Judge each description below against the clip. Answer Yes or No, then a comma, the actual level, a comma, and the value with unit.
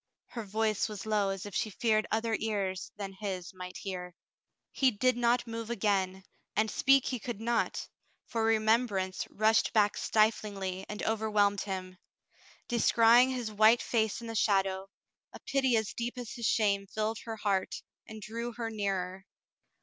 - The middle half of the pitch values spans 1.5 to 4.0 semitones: Yes, average, 2.7 semitones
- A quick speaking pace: No, average, 160 wpm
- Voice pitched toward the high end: Yes, high, 215 Hz